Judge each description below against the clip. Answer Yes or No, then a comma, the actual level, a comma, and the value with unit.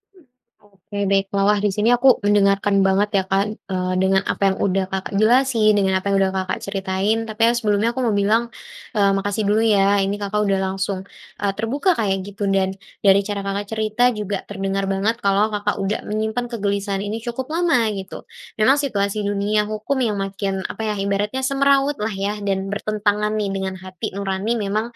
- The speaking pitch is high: Yes, high, 205 Hz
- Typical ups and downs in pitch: No, narrow, 1.9 semitones